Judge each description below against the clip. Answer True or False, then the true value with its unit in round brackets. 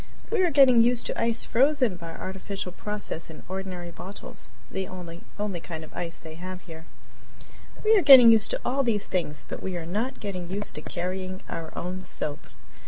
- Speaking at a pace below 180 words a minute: False (185 wpm)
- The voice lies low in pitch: False (190 Hz)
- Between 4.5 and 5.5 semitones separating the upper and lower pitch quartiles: True (4.8 semitones)